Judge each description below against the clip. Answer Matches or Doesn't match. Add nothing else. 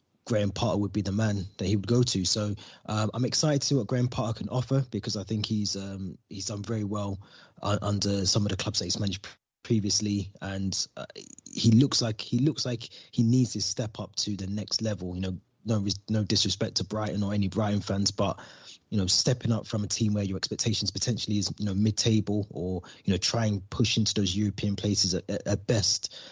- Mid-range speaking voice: Doesn't match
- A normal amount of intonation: Doesn't match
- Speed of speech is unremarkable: Doesn't match